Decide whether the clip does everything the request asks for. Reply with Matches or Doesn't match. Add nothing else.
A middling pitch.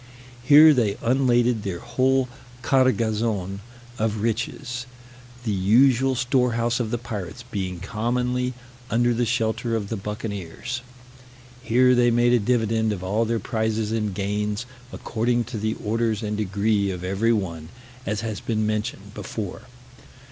Doesn't match